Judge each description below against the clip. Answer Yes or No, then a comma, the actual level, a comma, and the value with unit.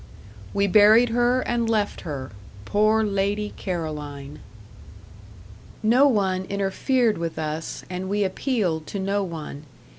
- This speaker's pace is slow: Yes, slow, 120 wpm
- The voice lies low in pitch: No, high, 200 Hz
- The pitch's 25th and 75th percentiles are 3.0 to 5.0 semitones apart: Yes, average, 4.7 semitones